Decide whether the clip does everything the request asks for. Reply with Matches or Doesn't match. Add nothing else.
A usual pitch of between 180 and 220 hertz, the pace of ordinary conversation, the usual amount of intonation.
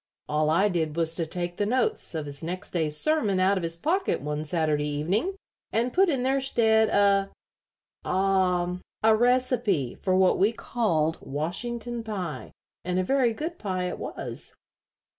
Doesn't match